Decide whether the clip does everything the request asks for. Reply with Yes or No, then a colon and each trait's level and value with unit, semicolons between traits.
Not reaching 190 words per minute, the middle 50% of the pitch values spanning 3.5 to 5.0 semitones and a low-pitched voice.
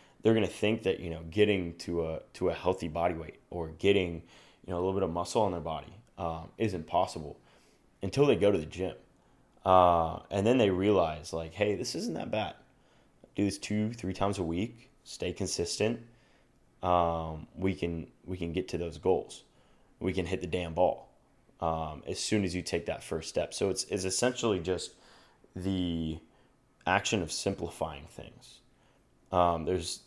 No: average, 180 wpm; average, 3.1 semitones; very low, 90 Hz